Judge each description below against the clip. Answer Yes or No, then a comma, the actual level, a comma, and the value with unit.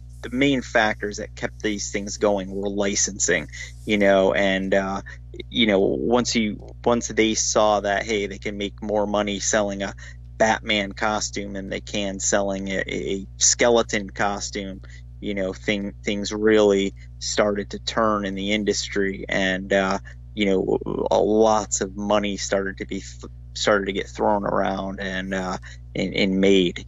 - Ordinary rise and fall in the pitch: No, narrow, 1.8 semitones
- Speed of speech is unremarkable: Yes, average, 160 wpm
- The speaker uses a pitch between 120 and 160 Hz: No, low, 100 Hz